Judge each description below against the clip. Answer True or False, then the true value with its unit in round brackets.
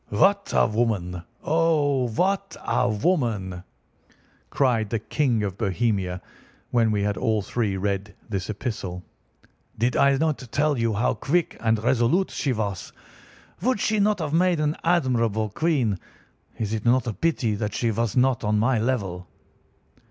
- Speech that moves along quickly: False (150 wpm)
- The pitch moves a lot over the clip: True (5.7 semitones)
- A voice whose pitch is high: False (115 Hz)